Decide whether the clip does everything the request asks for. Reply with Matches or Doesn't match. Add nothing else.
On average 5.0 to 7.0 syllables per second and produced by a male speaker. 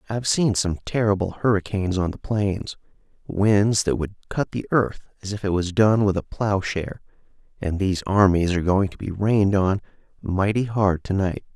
Matches